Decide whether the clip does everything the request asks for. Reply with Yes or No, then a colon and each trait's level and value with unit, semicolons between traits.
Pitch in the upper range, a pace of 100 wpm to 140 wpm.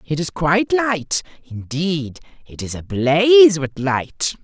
No: medium, 165 Hz; slow, 135 wpm